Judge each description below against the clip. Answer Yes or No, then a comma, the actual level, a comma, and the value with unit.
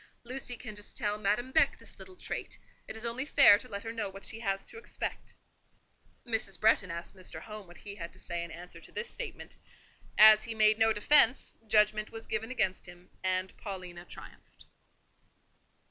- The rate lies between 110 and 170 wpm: No, average, 190 wpm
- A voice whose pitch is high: Yes, high, 210 Hz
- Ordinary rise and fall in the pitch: Yes, average, 3.2 semitones